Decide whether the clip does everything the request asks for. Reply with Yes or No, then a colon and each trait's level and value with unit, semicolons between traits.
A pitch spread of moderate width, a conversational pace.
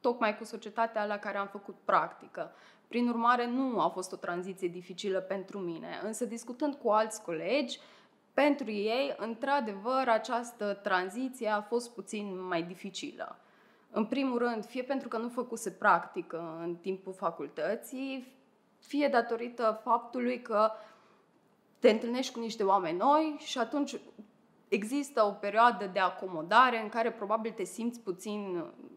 Yes: average, 3.5 semitones; average, 145 wpm